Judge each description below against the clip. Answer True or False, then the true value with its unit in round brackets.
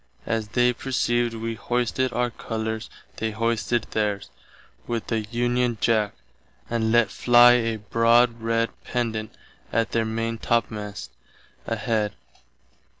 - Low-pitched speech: True (115 Hz)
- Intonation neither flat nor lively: False (1.4 semitones)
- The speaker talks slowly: True (115 wpm)